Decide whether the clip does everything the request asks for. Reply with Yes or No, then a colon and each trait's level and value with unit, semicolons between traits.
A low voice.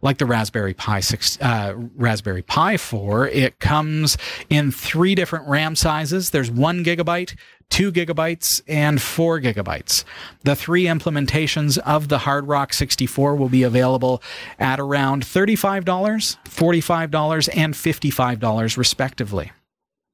No: medium, 145 Hz